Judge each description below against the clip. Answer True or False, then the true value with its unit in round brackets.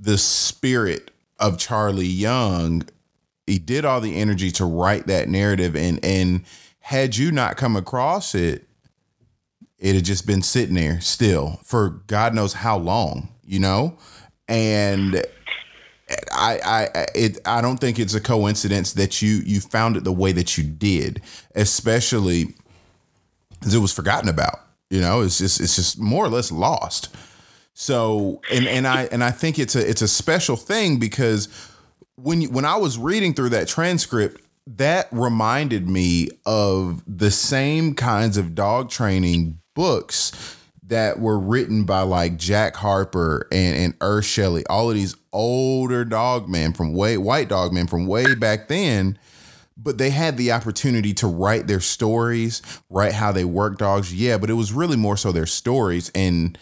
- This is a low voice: True (105 Hz)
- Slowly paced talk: False (165 wpm)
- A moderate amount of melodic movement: True (4.2 semitones)